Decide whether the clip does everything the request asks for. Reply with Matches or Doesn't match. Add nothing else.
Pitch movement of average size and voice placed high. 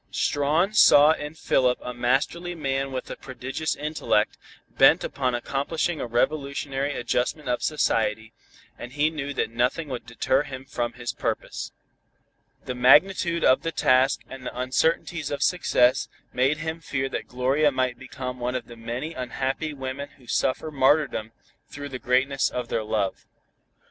Doesn't match